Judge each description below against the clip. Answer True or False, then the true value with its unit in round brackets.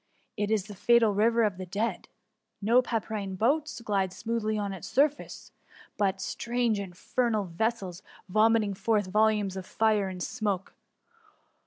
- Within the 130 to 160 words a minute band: True (145 wpm)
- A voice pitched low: False (210 Hz)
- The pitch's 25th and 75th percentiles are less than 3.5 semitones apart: True (2.8 semitones)